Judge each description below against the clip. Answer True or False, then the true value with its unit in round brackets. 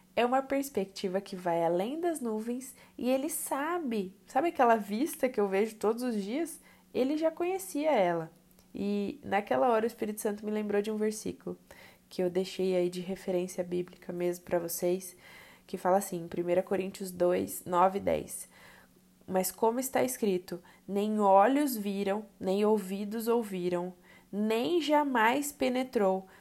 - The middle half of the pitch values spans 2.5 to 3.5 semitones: False (4.9 semitones)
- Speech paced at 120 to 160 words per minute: True (150 wpm)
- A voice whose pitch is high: True (205 Hz)